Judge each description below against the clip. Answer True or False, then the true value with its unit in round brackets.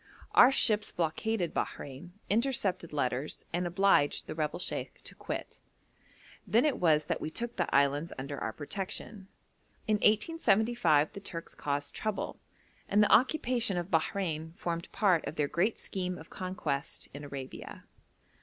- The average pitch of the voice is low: False (175 Hz)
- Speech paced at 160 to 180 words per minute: False (145 wpm)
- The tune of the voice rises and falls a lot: True (5.7 semitones)